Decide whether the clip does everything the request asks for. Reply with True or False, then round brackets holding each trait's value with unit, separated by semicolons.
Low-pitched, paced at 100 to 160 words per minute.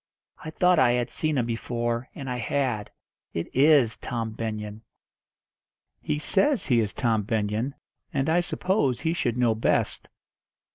True (125 Hz; 150 wpm)